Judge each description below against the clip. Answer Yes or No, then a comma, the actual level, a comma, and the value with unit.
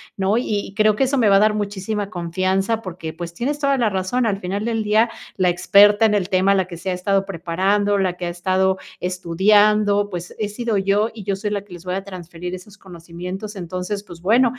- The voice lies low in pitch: No, high, 195 Hz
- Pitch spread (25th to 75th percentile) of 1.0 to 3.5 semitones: Yes, narrow, 2.5 semitones